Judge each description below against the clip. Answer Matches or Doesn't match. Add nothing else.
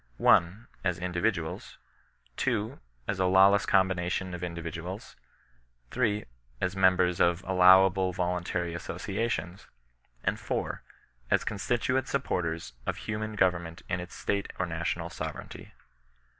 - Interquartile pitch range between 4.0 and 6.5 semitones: Doesn't match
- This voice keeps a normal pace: Doesn't match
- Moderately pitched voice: Doesn't match